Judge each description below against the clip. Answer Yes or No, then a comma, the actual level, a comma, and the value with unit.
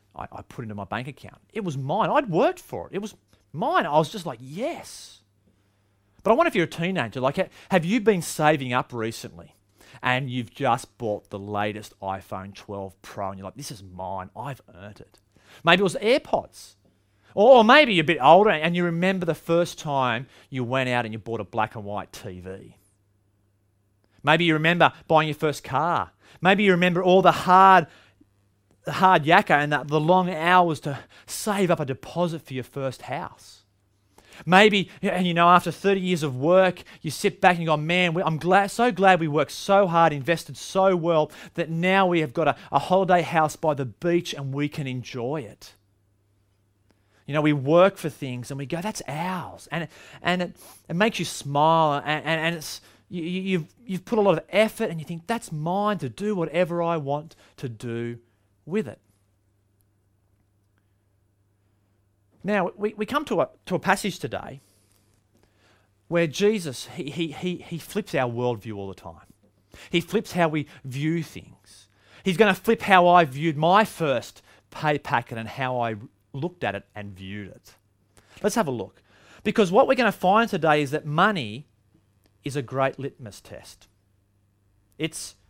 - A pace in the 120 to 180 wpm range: No, average, 190 wpm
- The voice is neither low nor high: Yes, medium, 145 Hz